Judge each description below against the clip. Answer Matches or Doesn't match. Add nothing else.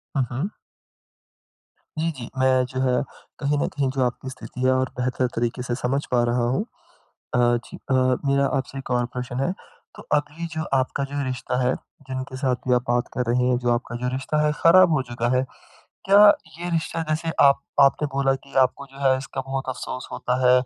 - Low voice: Matches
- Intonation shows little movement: Matches